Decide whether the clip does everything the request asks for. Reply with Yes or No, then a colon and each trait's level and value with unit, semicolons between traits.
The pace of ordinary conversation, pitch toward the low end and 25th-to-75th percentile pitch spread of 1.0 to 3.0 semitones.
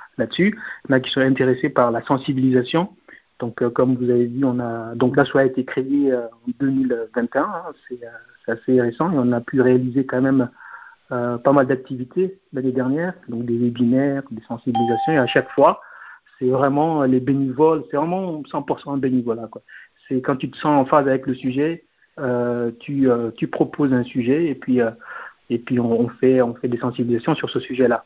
Yes: average, 205 wpm; low, 130 Hz; narrow, 2.6 semitones